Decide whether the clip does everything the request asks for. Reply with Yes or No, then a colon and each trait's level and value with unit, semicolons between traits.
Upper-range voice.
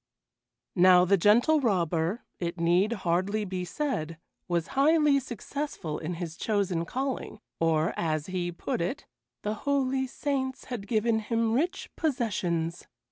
Yes: high, 200 Hz